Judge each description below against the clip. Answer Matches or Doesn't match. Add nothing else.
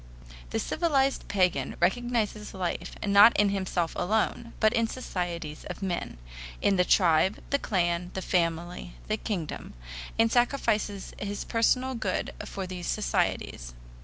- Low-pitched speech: Doesn't match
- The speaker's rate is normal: Doesn't match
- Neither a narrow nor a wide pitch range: Matches